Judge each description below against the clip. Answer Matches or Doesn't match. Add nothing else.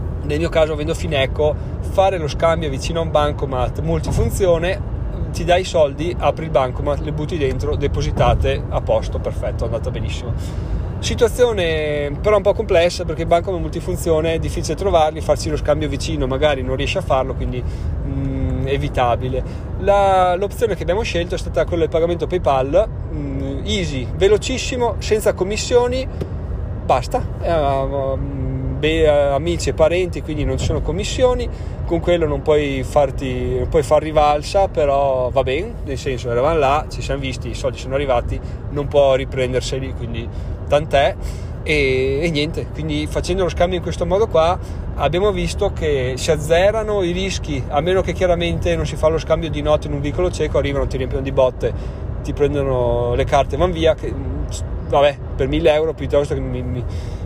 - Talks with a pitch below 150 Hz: Matches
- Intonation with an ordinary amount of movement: Matches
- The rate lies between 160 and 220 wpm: Matches